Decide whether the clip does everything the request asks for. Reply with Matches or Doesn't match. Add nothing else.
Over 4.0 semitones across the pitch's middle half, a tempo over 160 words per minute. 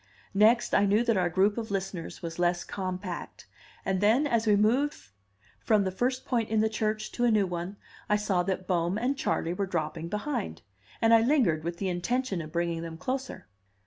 Matches